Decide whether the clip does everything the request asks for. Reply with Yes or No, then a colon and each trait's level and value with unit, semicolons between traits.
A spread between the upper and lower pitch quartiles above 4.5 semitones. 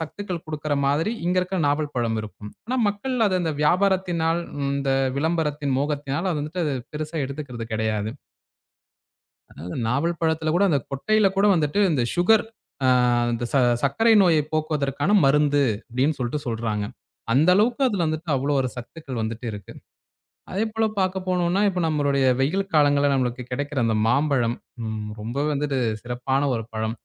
Yes: average, 5.1 semitones